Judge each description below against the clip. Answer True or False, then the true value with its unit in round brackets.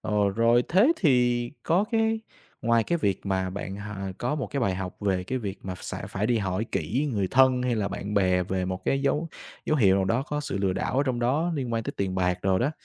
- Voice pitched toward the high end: False (110 Hz)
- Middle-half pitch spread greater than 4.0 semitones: True (5.4 semitones)